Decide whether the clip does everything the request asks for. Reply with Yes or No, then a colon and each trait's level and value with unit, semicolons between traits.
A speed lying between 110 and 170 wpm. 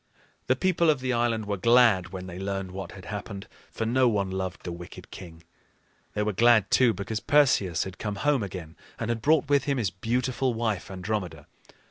No: average, 195 wpm